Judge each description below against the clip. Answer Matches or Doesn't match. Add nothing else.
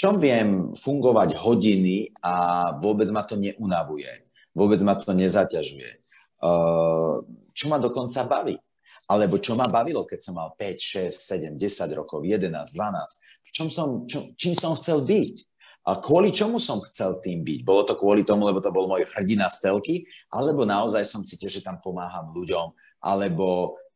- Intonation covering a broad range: Matches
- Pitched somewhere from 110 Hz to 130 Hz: Doesn't match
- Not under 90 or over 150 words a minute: Doesn't match